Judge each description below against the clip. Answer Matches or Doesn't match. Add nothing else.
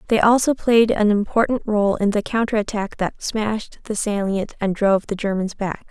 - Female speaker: Matches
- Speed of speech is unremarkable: Matches